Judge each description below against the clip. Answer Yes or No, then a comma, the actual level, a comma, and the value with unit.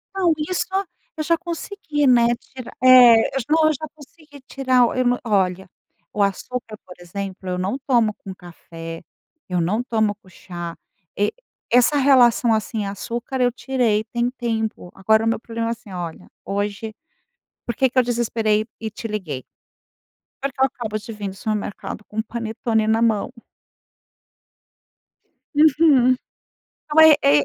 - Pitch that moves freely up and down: No, average, 4.0 semitones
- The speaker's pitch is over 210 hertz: Yes, high, 230 Hz